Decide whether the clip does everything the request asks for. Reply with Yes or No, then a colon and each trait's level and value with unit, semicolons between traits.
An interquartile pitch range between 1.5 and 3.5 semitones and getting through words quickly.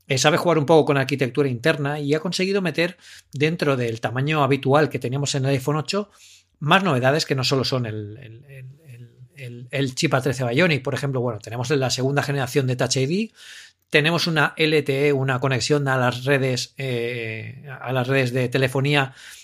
No: average, 2.7 semitones; average, 190 wpm